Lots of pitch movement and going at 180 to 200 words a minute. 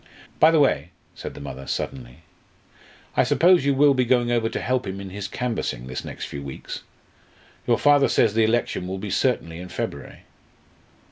Yes: wide, 7.4 semitones; average, 185 wpm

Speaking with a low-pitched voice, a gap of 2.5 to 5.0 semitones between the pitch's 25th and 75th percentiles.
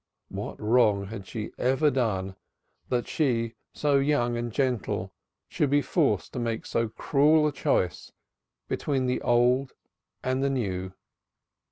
Yes: low, 125 Hz; average, 3.8 semitones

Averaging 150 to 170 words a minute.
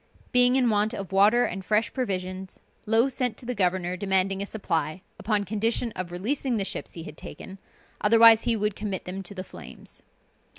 No: average, 185 wpm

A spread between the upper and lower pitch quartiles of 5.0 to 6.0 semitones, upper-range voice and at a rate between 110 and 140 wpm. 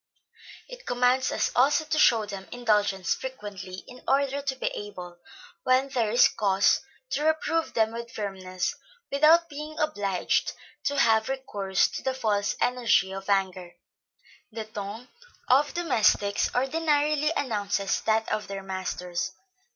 Yes: wide, 5.5 semitones; high, 225 Hz; slow, 135 wpm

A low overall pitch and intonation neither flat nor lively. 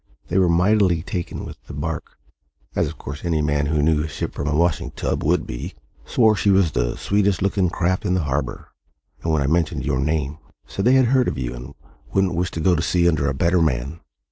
Yes: very low, 80 Hz; average, 3.9 semitones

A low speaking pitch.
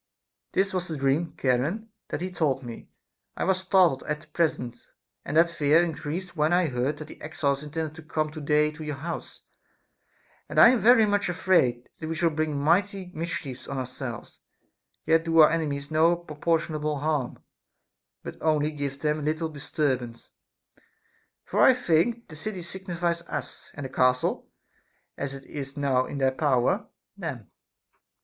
No: medium, 155 Hz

